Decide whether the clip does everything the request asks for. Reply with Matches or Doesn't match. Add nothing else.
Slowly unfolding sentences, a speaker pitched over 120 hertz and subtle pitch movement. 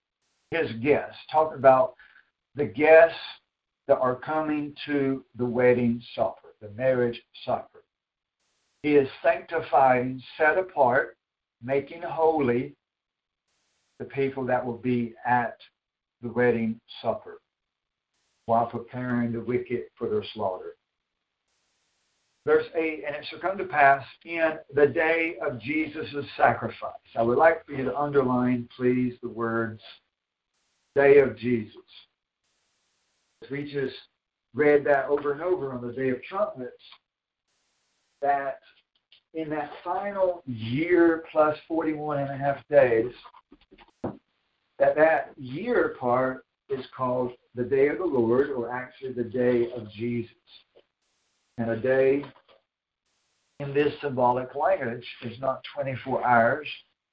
Doesn't match